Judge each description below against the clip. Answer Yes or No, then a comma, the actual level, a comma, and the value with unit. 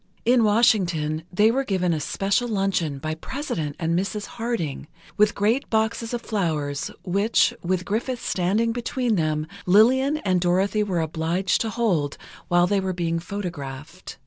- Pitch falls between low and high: No, high, 195 Hz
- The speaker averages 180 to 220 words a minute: No, average, 150 wpm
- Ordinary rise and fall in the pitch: Yes, average, 5.0 semitones